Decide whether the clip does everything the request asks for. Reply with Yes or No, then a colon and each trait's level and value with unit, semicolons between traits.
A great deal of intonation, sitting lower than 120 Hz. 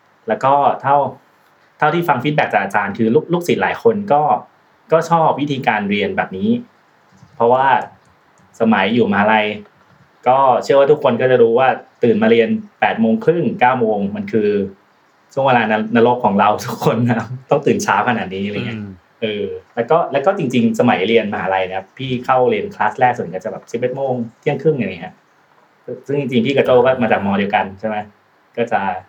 No: wide, 7.3 semitones; low, 125 Hz